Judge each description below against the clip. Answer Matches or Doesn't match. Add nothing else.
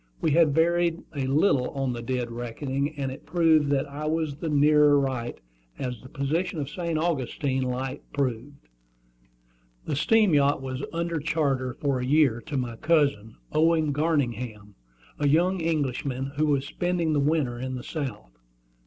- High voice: Doesn't match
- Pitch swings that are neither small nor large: Matches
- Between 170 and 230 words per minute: Doesn't match